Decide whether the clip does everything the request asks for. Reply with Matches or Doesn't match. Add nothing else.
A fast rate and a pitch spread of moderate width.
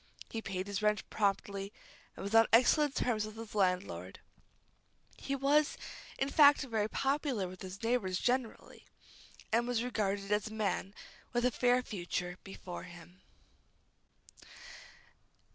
Doesn't match